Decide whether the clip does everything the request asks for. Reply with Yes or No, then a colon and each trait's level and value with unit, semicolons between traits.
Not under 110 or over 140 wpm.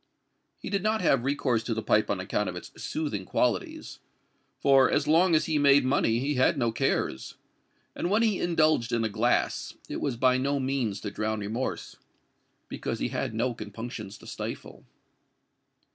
No: average, 170 wpm